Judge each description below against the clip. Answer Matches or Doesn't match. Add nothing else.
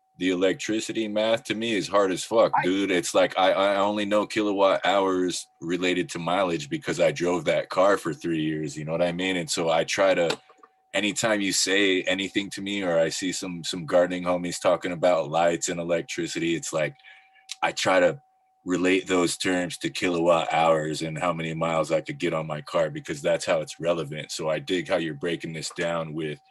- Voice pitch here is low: Matches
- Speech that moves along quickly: Matches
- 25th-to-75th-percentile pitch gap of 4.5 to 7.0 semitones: Doesn't match